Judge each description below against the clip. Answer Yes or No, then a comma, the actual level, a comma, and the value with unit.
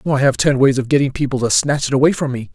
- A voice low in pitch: Yes, low, 130 Hz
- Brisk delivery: Yes, fast, 305 wpm